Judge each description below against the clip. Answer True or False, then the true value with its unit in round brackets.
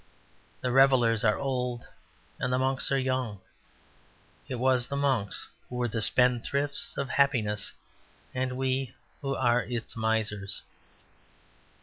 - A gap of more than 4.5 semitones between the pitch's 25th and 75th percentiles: False (2.5 semitones)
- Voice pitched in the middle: False (125 Hz)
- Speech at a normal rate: False (125 wpm)